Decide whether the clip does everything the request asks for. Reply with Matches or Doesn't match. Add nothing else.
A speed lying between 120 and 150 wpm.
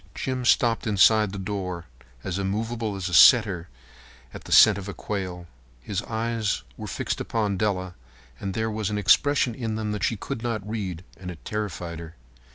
Doesn't match